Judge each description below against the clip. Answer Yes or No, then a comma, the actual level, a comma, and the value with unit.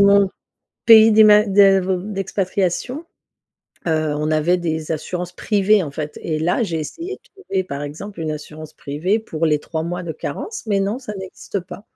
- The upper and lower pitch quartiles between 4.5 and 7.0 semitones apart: Yes, average, 4.8 semitones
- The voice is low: No, medium, 185 Hz